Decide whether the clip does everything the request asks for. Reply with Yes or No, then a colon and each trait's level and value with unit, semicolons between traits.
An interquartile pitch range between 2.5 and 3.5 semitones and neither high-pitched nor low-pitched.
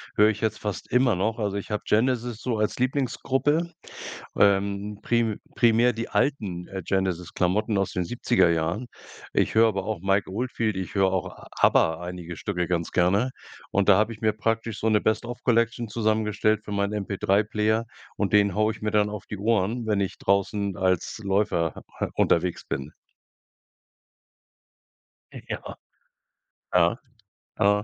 No: average, 2.8 semitones; low, 105 Hz